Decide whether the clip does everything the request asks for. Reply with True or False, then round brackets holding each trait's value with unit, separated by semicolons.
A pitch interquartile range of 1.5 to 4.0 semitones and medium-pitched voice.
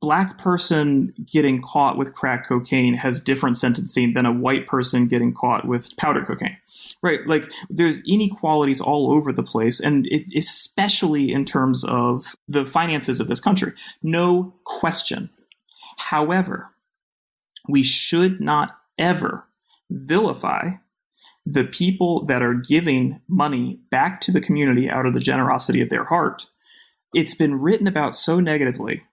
False (5.4 semitones; 150 Hz)